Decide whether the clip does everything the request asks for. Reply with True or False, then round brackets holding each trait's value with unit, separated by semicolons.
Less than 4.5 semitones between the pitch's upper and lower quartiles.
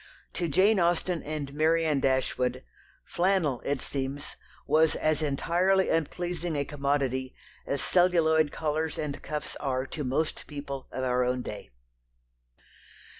True (3.4 semitones)